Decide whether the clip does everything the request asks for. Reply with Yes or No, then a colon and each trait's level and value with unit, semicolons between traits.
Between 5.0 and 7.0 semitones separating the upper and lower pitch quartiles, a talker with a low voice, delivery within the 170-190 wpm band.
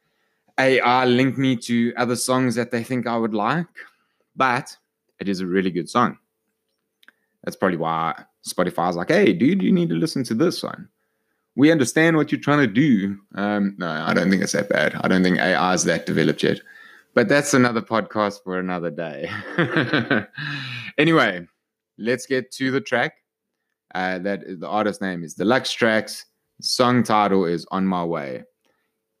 Yes: average, 5.3 semitones; low, 110 Hz; average, 175 wpm